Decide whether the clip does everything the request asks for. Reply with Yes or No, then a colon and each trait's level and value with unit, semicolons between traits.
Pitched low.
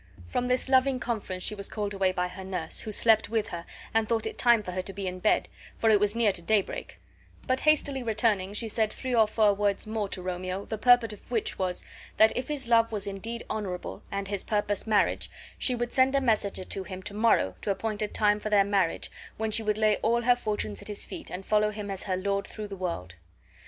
No: high, 210 Hz